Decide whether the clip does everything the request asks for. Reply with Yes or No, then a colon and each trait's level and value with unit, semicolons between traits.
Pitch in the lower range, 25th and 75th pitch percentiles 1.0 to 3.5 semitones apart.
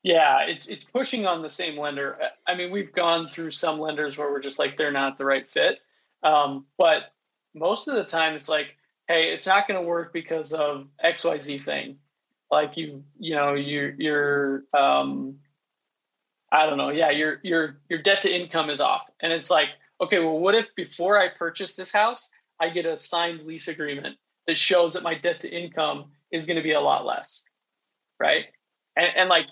No: medium, 160 Hz; average, 2.9 semitones